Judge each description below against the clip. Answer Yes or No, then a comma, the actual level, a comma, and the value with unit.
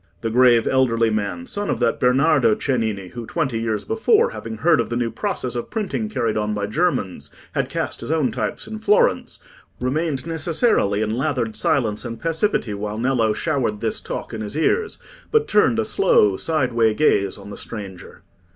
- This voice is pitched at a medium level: No, low, 125 Hz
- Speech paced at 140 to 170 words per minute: No, average, 180 wpm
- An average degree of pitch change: No, wide, 7.1 semitones